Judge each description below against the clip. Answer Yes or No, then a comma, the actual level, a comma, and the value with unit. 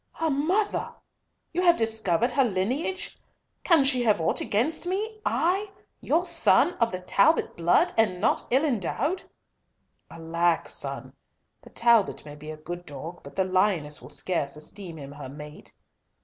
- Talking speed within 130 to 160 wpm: Yes, average, 155 wpm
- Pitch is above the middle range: Yes, high, 210 Hz